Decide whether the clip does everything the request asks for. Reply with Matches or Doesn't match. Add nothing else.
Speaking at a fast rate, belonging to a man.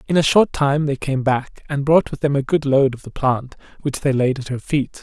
Matches